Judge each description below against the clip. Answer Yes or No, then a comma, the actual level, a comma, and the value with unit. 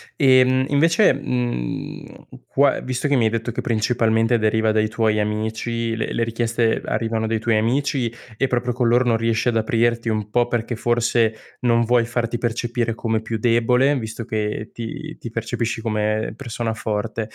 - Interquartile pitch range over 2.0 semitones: No, narrow, 1.6 semitones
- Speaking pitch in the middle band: No, low, 115 Hz